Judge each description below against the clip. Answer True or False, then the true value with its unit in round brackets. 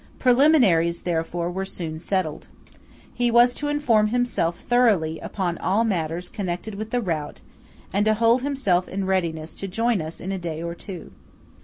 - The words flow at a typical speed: True (165 wpm)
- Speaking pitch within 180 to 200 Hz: True (190 Hz)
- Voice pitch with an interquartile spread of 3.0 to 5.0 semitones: False (5.4 semitones)